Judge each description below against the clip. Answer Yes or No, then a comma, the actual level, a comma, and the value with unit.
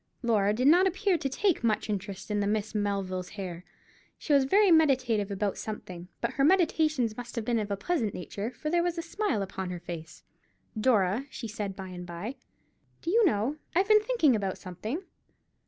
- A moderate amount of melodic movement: No, wide, 7.5 semitones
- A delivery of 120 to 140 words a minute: No, average, 195 wpm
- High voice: Yes, high, 220 Hz